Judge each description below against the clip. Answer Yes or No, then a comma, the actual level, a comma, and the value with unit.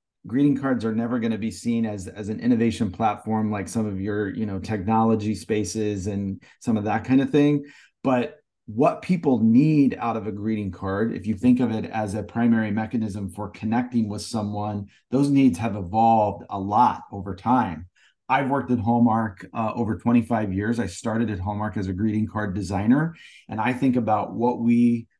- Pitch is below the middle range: Yes, low, 110 Hz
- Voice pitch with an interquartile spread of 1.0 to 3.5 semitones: Yes, narrow, 2.6 semitones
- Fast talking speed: No, average, 195 wpm